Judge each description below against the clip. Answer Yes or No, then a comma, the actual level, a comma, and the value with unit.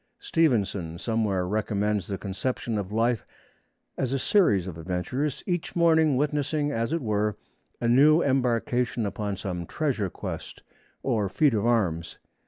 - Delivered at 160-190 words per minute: No, average, 140 wpm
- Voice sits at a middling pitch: No, low, 115 Hz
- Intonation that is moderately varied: No, wide, 5.7 semitones